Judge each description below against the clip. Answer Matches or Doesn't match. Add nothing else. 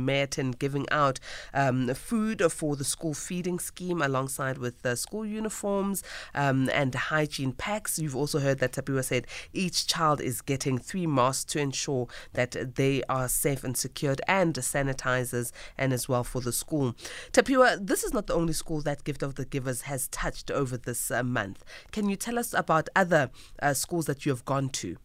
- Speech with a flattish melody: Doesn't match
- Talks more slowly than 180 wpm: Doesn't match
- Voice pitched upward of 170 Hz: Doesn't match